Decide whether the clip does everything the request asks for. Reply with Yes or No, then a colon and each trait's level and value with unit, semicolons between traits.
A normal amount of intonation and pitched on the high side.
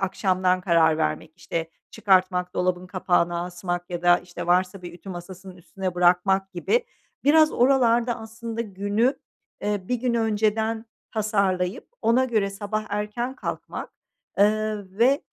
Yes: average, 3.8 semitones; high, 195 Hz